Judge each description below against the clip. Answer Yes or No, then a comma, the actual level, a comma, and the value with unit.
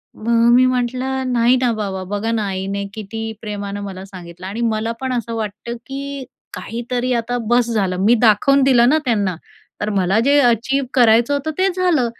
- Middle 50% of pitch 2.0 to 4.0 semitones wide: Yes, average, 3.6 semitones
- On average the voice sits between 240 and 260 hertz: No, high, 230 Hz